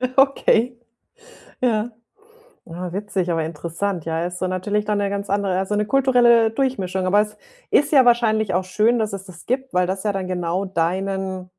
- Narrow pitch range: No, average, 3.4 semitones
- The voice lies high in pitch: Yes, high, 200 Hz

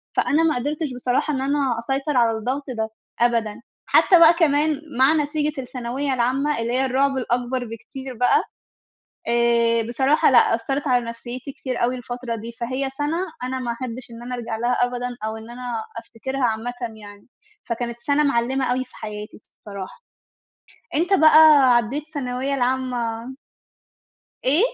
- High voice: Yes, very high, 250 Hz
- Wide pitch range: No, average, 2.9 semitones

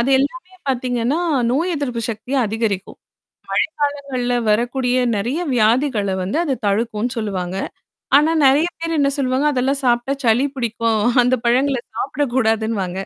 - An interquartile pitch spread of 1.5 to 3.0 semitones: No, average, 3.8 semitones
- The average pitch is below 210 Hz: No, high, 245 Hz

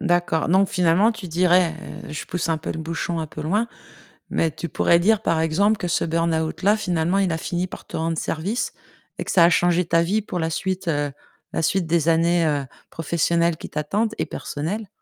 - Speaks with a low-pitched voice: No, medium, 170 Hz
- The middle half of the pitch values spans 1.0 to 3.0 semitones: Yes, narrow, 2.5 semitones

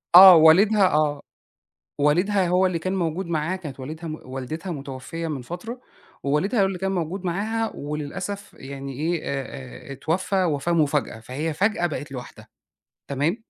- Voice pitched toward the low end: No, medium, 165 Hz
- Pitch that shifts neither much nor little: Yes, average, 4.7 semitones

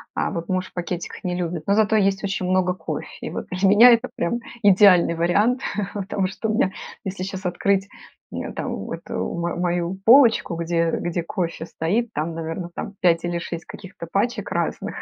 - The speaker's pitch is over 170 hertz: Yes, medium, 185 Hz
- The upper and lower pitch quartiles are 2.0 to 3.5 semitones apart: Yes, average, 2.8 semitones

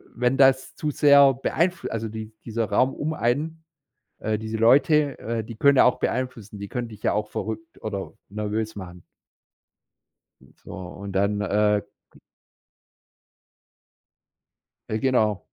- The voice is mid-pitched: No, low, 115 Hz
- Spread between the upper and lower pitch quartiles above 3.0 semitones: Yes, average, 4.1 semitones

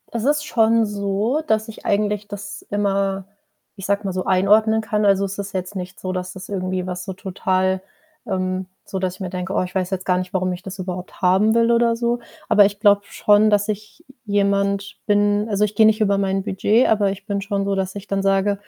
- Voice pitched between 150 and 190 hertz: No, high, 200 Hz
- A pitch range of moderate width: No, narrow, 1.9 semitones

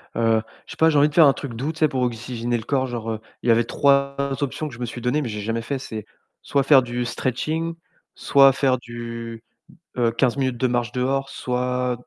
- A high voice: No, low, 125 Hz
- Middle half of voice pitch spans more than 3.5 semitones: No, average, 2.8 semitones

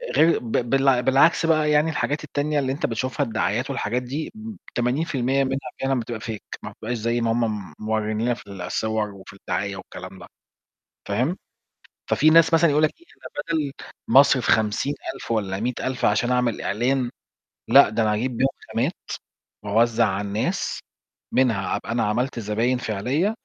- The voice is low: Yes, low, 120 Hz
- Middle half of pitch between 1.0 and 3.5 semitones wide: No, average, 4.0 semitones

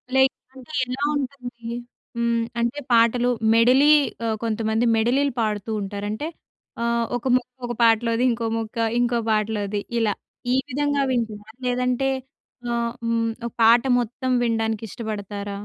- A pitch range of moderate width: No, narrow, 2.1 semitones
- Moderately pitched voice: No, high, 235 Hz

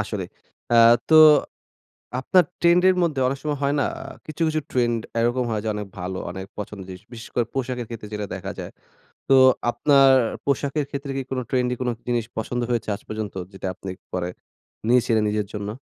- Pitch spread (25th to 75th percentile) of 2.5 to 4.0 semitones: No, average, 4.7 semitones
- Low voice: Yes, low, 120 Hz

